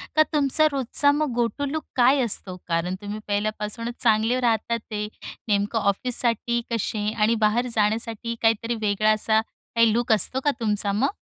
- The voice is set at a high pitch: Yes, high, 225 Hz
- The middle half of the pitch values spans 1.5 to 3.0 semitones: Yes, narrow, 2.5 semitones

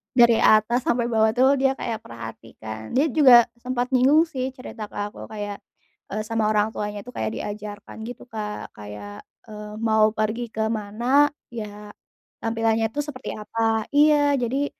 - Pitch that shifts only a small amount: No, average, 3.2 semitones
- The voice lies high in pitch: Yes, high, 225 Hz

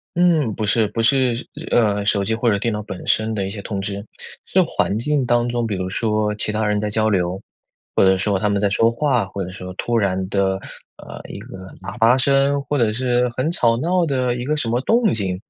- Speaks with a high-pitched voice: No, low, 110 Hz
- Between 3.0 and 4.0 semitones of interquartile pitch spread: Yes, average, 3.7 semitones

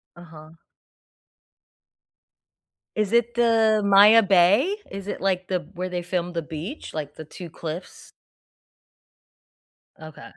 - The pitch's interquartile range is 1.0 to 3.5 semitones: No, average, 4.2 semitones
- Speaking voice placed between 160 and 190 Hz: Yes, medium, 185 Hz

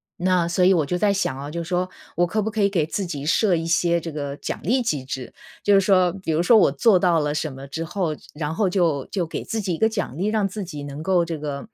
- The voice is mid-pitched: Yes, medium, 170 Hz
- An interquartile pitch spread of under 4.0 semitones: No, average, 4.3 semitones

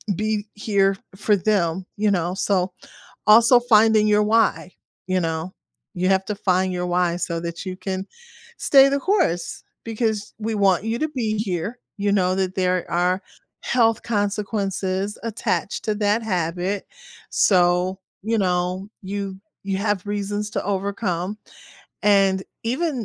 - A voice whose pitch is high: Yes, high, 200 Hz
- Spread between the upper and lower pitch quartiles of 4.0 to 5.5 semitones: No, narrow, 2.6 semitones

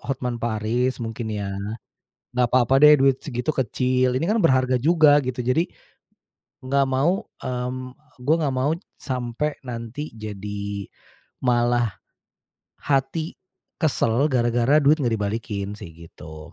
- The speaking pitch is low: Yes, low, 125 Hz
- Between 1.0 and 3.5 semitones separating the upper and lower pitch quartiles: Yes, average, 3.1 semitones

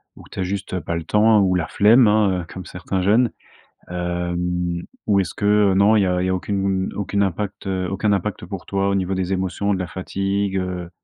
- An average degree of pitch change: No, narrow, 1.9 semitones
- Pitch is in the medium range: No, very low, 95 Hz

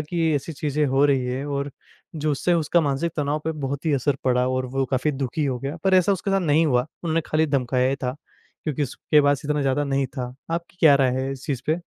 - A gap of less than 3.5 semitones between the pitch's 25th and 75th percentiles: Yes, average, 2.9 semitones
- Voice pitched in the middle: Yes, medium, 145 Hz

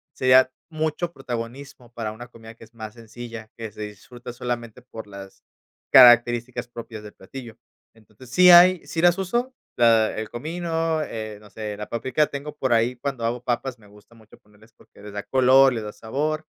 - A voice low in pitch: Yes, low, 120 Hz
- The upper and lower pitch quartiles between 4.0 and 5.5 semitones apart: No, average, 3.5 semitones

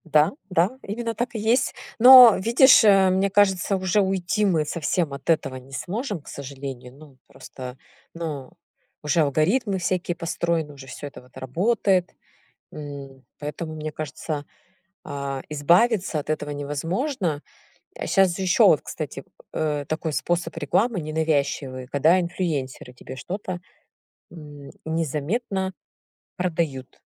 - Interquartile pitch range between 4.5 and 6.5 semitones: Yes, average, 4.9 semitones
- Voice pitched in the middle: Yes, medium, 165 Hz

